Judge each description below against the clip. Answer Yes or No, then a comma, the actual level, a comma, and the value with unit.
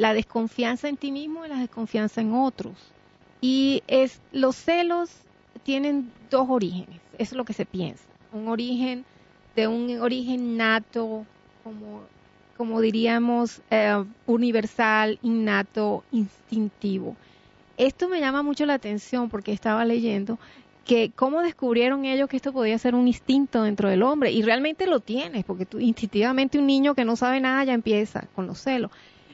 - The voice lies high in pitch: Yes, high, 235 Hz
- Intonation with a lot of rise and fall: No, average, 3.2 semitones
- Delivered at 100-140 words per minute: No, average, 155 wpm